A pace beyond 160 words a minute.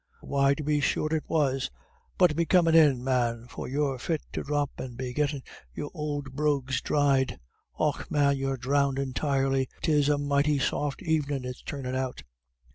Yes: average, 170 wpm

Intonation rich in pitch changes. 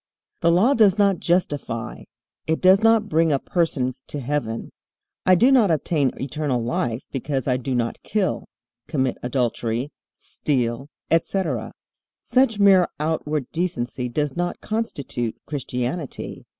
Yes: wide, 6.5 semitones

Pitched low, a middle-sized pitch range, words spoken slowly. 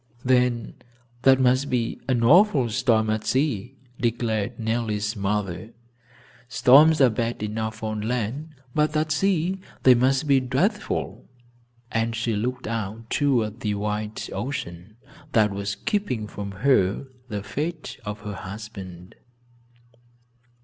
Yes: low, 115 Hz; average, 3.9 semitones; slow, 125 wpm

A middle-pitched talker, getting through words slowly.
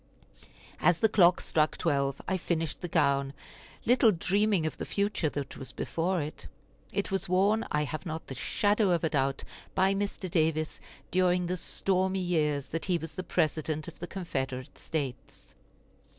No: medium, 165 Hz; average, 165 wpm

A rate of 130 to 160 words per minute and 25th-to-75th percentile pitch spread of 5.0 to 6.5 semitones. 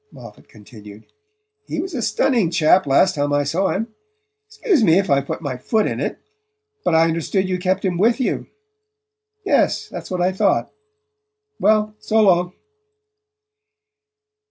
Yes: average, 155 wpm; wide, 5.6 semitones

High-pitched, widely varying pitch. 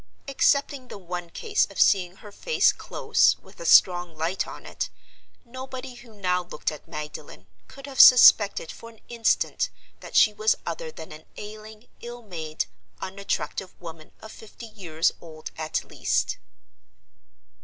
Yes: high, 205 Hz; wide, 6.1 semitones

